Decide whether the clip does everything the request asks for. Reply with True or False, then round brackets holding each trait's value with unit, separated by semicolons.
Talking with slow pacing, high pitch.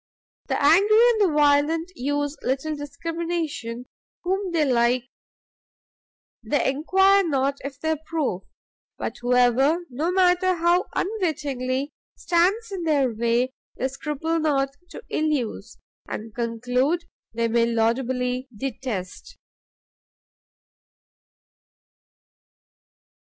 True (100 wpm; 290 Hz)